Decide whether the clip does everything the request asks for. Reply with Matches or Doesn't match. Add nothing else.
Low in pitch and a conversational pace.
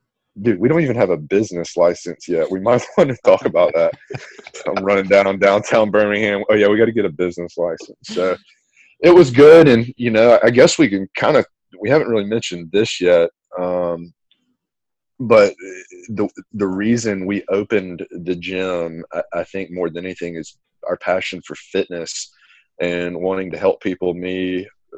Matches